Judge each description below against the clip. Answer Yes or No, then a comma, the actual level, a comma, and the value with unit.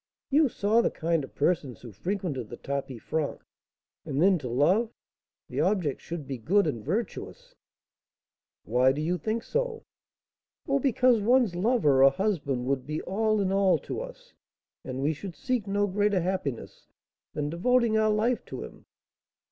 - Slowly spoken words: No, average, 170 wpm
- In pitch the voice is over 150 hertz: Yes, medium, 185 Hz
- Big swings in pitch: Yes, wide, 7.6 semitones